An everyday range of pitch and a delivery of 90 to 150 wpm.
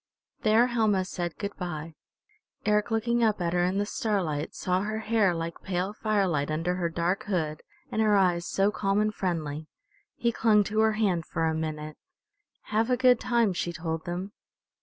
No: average, 4.2 semitones; average, 180 wpm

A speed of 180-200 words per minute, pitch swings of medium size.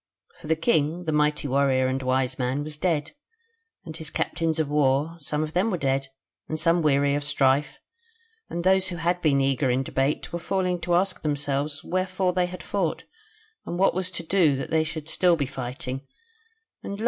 Yes: average, 195 wpm; average, 4.0 semitones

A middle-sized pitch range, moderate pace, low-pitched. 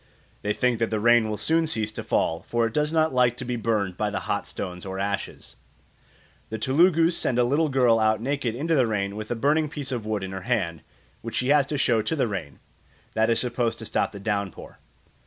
No: average, 4.4 semitones; fast, 230 wpm; low, 115 Hz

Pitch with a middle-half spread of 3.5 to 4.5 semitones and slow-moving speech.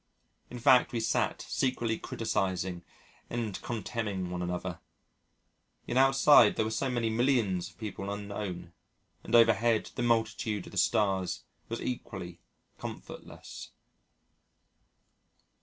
Yes: average, 3.9 semitones; slow, 115 wpm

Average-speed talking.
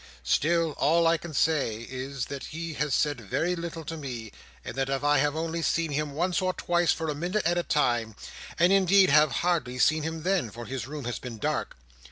No: fast, 215 wpm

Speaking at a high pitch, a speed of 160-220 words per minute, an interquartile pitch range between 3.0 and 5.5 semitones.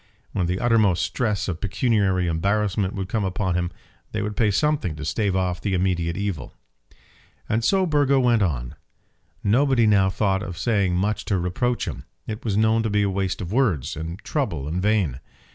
No: low, 100 Hz; average, 180 wpm; average, 3.5 semitones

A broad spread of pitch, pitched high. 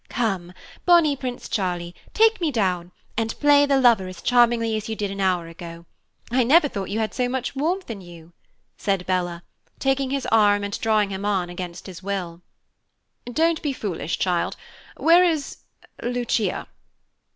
Yes: wide, 6.4 semitones; high, 215 Hz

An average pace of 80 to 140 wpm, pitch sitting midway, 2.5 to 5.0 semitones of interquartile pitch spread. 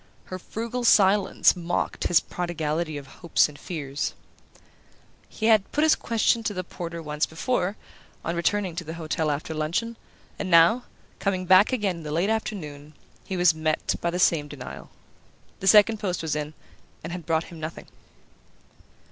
No: average, 165 wpm; medium, 175 Hz; average, 4.3 semitones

